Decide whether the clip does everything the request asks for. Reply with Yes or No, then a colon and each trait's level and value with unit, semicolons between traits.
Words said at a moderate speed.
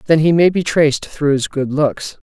No: fast, 240 wpm